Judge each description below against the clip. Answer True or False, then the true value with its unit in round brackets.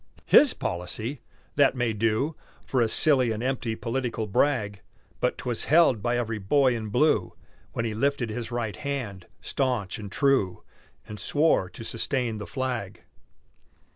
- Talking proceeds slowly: False (150 wpm)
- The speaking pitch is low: True (120 Hz)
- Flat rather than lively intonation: False (3.8 semitones)